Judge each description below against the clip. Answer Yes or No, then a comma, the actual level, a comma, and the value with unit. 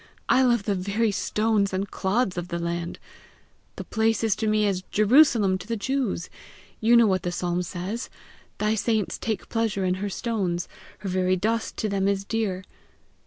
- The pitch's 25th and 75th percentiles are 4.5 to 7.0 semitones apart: No, average, 3.2 semitones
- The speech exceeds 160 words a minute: Yes, average, 180 wpm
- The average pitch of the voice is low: No, high, 200 Hz